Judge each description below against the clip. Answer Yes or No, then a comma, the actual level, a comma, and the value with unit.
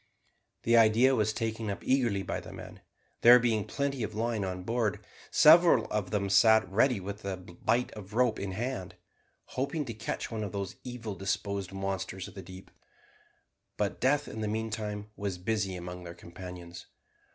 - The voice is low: Yes, low, 105 Hz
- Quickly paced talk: No, average, 175 wpm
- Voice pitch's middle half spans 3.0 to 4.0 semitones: Yes, average, 3.3 semitones